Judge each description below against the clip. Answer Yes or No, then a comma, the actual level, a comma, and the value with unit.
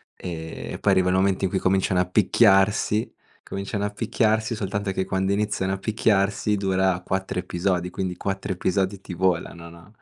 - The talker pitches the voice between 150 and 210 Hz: No, very low, 95 Hz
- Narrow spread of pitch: Yes, narrow, 1.8 semitones